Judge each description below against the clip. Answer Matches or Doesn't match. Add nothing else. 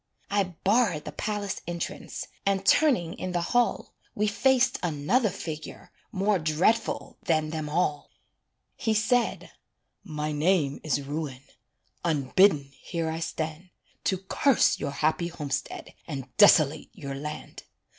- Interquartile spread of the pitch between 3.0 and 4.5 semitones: Doesn't match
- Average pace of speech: Doesn't match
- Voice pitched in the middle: Matches